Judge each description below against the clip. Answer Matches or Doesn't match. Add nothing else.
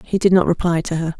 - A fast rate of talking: Matches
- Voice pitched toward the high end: Doesn't match